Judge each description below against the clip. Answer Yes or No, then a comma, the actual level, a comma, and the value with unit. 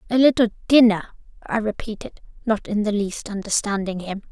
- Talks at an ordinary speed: Yes, average, 155 wpm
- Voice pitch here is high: Yes, high, 215 Hz